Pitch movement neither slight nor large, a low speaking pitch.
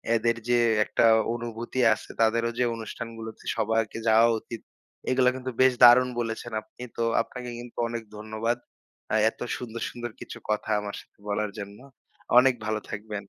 No: narrow, 1.8 semitones; low, 115 Hz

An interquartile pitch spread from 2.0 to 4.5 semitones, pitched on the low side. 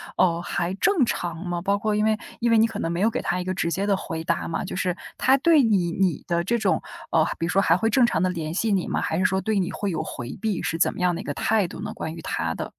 No: average, 4.2 semitones; high, 190 Hz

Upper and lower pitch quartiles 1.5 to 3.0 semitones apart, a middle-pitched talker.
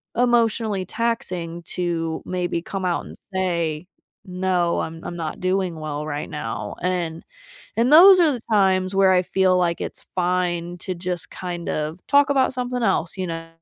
Yes: narrow, 2.6 semitones; medium, 180 Hz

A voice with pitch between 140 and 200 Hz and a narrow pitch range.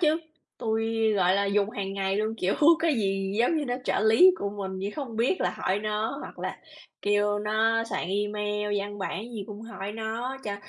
No: high, 210 Hz; narrow, 2.1 semitones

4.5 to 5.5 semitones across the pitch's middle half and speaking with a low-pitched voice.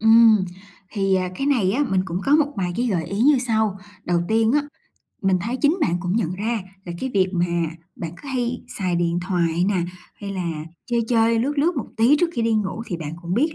No: average, 5.2 semitones; high, 215 Hz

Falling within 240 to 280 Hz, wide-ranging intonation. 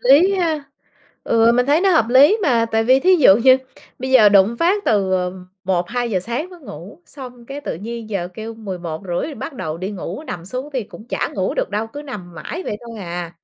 No: high, 230 Hz; wide, 6.3 semitones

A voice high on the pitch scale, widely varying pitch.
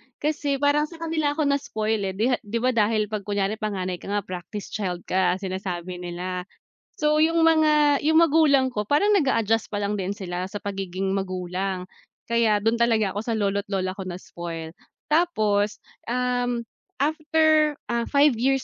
Yes: high, 215 Hz; wide, 7.0 semitones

